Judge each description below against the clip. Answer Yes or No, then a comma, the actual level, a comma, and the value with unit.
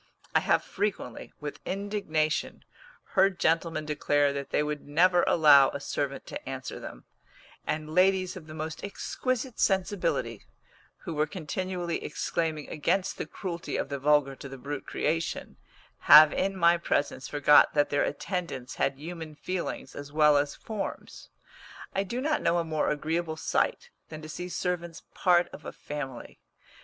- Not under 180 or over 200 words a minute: No, average, 155 wpm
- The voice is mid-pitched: Yes, medium, 160 Hz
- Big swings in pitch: No, average, 3.8 semitones